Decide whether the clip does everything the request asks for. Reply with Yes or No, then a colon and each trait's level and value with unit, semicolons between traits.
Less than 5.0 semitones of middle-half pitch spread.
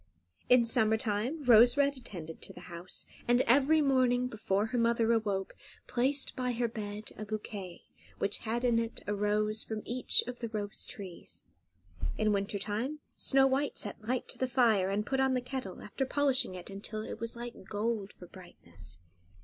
Yes: average, 3.5 semitones